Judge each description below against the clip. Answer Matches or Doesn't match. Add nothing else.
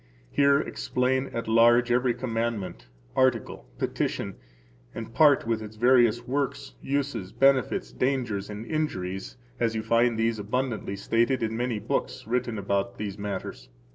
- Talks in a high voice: Doesn't match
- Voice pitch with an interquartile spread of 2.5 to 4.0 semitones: Matches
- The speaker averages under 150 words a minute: Matches